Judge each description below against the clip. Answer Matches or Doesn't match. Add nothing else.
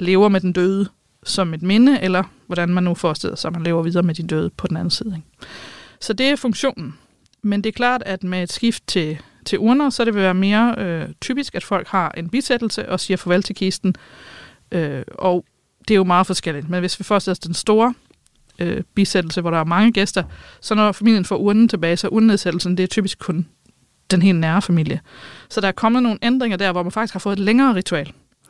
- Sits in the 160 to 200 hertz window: Matches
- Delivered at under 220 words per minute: Doesn't match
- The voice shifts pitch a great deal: Doesn't match